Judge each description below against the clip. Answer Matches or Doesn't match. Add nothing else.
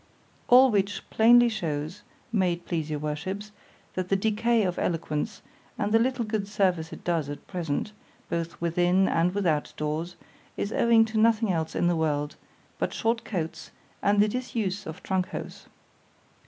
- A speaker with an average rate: Matches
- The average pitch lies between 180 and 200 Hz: Matches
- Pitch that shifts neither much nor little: Matches